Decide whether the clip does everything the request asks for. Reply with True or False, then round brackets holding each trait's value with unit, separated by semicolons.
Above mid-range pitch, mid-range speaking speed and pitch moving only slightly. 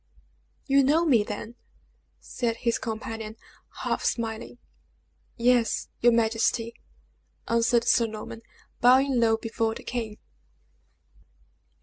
False (230 Hz; 100 wpm; 1.6 semitones)